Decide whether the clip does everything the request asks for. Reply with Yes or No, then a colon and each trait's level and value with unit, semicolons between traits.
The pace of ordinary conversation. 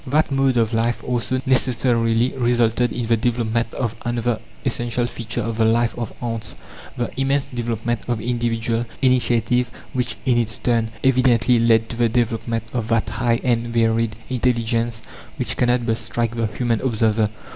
Yes: average, 160 wpm